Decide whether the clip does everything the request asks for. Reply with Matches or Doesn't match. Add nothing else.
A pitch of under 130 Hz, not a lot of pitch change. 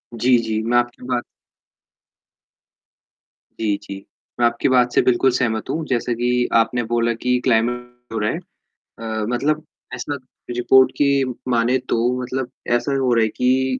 Matches